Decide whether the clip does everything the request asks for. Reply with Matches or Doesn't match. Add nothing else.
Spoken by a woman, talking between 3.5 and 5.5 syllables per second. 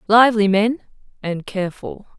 Matches